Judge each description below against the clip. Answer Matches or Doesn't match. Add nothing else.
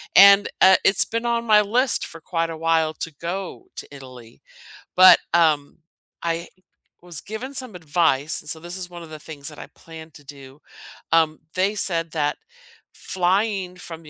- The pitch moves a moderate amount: Matches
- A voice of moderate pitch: Matches